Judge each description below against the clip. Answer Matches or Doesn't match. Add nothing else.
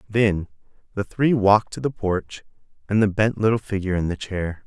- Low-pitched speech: Matches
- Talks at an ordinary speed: Matches